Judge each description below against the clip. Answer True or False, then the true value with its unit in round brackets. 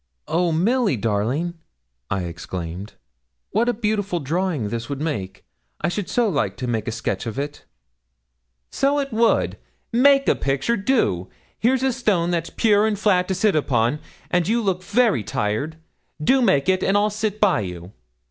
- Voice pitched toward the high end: False (175 Hz)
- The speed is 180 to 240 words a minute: False (170 wpm)